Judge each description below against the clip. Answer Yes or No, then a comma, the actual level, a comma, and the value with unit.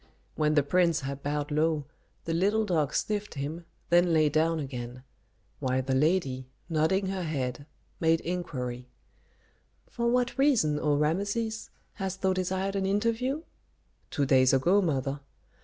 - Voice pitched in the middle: Yes, medium, 160 Hz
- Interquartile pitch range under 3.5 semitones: No, average, 5.3 semitones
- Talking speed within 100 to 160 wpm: Yes, average, 140 wpm